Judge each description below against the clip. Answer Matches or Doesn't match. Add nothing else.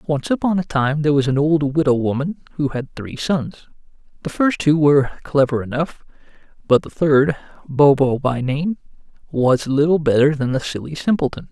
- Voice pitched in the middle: Matches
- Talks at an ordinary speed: Matches